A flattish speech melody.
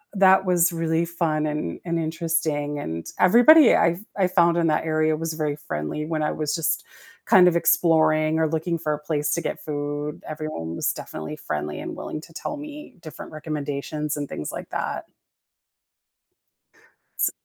Yes: narrow, 2.1 semitones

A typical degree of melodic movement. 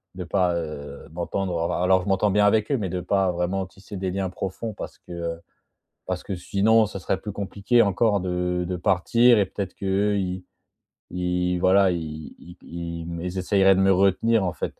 No: narrow, 1.9 semitones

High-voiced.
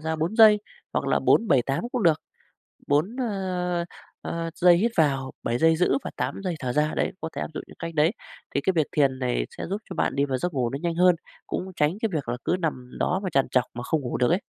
No: medium, 160 Hz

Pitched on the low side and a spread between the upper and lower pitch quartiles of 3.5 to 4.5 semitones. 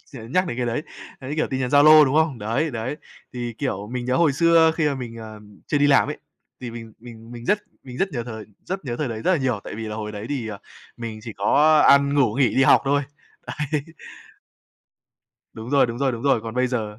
Yes: low, 125 Hz; average, 4.0 semitones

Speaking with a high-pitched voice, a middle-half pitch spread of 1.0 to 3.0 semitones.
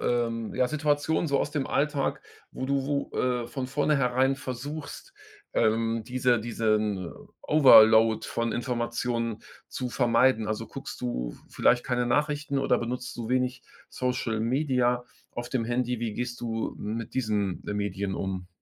No: low, 120 Hz; average, 2.7 semitones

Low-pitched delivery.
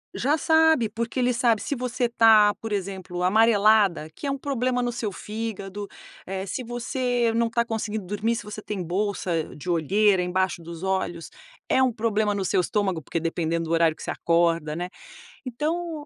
No: high, 210 Hz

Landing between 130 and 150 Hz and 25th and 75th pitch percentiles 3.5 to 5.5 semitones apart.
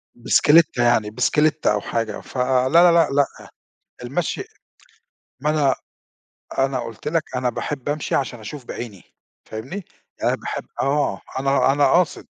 Yes: low, 135 Hz; average, 3.9 semitones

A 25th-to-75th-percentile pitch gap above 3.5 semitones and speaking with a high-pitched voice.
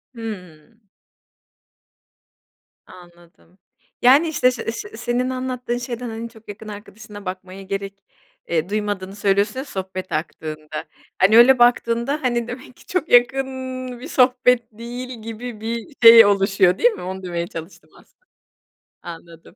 Yes: average, 4.6 semitones; high, 220 Hz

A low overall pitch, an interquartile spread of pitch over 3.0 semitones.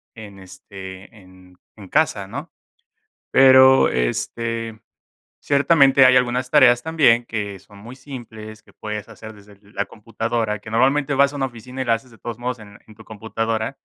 Yes: low, 115 Hz; average, 3.8 semitones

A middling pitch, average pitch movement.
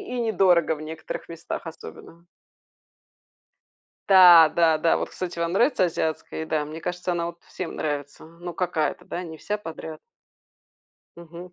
No: medium, 170 Hz; narrow, 2.0 semitones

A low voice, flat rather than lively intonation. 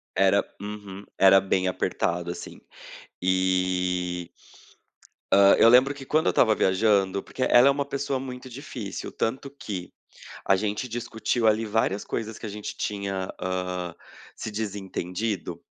No: low, 105 Hz; average, 3.9 semitones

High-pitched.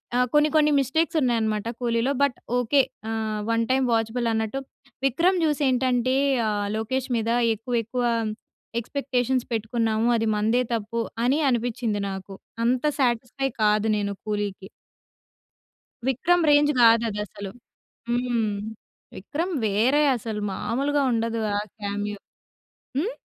Yes: high, 235 Hz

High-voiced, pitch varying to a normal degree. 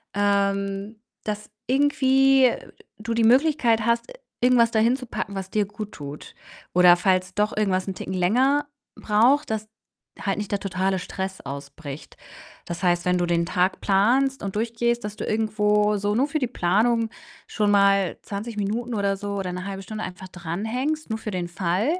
Yes: high, 205 Hz; average, 3.7 semitones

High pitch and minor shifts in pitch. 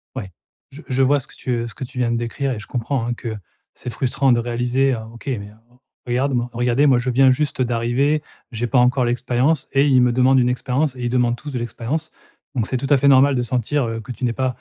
No: low, 125 Hz; narrow, 2.0 semitones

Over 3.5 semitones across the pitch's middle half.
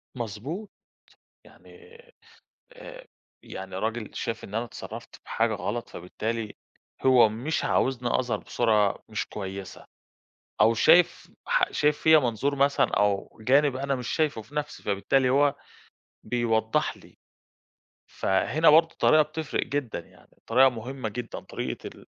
Yes: average, 4.8 semitones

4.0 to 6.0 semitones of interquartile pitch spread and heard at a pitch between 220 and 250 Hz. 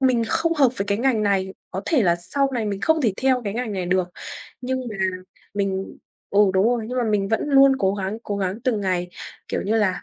No: average, 4.7 semitones; high, 210 Hz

